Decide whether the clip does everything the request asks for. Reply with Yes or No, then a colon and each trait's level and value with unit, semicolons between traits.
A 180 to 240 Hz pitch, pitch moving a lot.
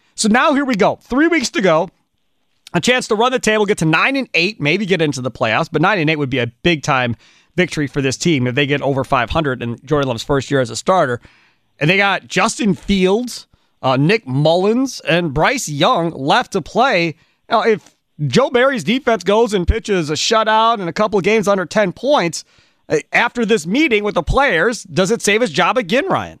Yes: medium, 185 Hz; wide, 7.4 semitones